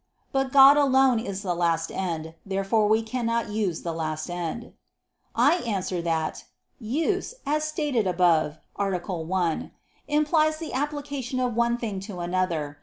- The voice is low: No, high, 210 Hz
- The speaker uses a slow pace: No, average, 145 wpm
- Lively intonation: Yes, wide, 7.4 semitones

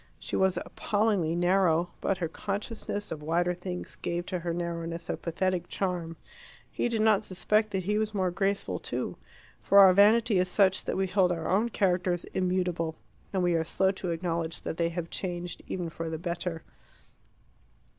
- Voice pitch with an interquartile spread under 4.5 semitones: Yes, narrow, 2.4 semitones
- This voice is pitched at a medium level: Yes, medium, 180 Hz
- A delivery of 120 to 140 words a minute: No, average, 175 wpm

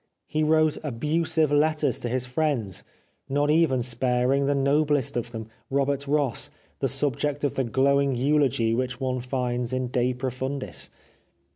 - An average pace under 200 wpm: Yes, average, 150 wpm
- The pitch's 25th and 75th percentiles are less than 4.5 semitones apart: Yes, average, 2.8 semitones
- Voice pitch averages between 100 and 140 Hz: Yes, low, 135 Hz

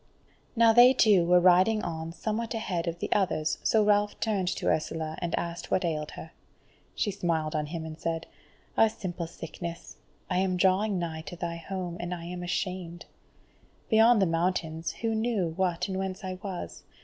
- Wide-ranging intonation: No, average, 3.4 semitones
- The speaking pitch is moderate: Yes, medium, 180 Hz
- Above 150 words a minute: Yes, average, 180 wpm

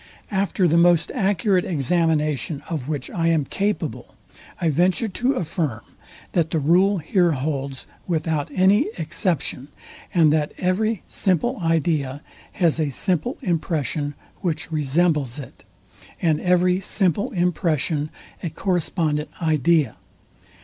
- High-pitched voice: No, medium, 165 Hz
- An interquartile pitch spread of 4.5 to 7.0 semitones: No, average, 3.4 semitones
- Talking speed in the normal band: No, slow, 120 wpm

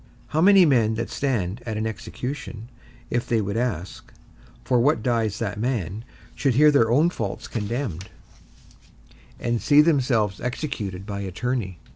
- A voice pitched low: Yes, low, 115 Hz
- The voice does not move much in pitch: No, average, 4.0 semitones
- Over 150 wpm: No, average, 145 wpm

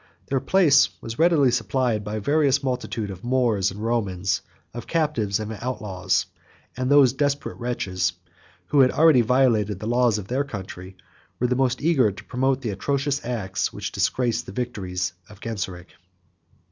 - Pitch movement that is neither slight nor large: Yes, average, 4.6 semitones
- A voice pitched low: Yes, low, 120 Hz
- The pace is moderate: Yes, average, 160 wpm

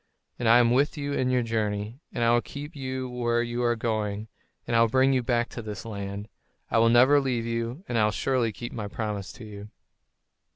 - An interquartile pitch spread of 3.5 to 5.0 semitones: No, narrow, 2.6 semitones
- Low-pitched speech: Yes, low, 120 Hz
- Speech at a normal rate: No, fast, 220 wpm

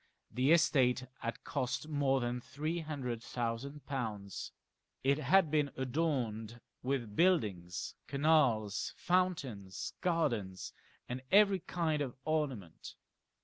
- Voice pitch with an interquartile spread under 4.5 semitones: No, average, 5.1 semitones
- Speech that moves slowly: Yes, slow, 105 wpm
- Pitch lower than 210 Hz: Yes, low, 135 Hz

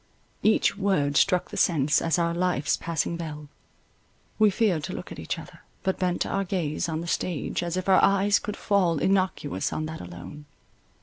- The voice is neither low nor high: Yes, medium, 170 Hz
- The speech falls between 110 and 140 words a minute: No, average, 185 wpm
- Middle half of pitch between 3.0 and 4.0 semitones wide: Yes, average, 3.7 semitones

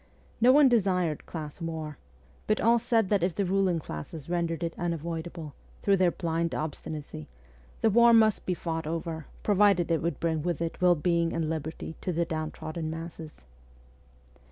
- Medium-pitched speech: Yes, medium, 170 Hz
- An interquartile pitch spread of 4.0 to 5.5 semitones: No, average, 2.7 semitones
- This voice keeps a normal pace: Yes, average, 165 wpm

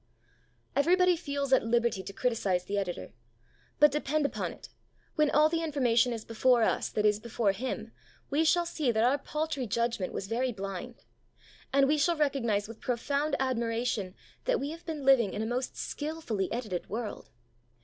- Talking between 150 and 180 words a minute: Yes, average, 170 wpm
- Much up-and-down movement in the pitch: No, average, 5.0 semitones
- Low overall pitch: No, very high, 250 Hz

